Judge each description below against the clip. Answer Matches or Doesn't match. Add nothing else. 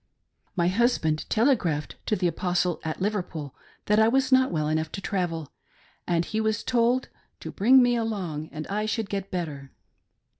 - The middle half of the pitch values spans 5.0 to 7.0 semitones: Matches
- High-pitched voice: Matches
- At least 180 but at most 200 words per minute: Doesn't match